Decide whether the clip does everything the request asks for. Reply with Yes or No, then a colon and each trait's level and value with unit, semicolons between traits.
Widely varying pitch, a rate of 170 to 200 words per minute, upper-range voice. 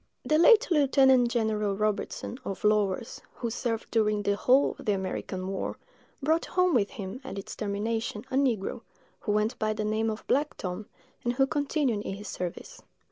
No: average, 4.4 semitones; average, 180 wpm; high, 220 Hz